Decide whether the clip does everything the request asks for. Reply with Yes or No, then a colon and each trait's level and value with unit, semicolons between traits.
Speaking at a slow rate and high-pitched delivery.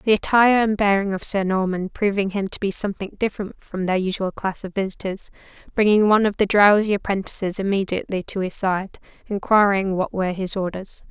No: average, 185 wpm; high, 195 Hz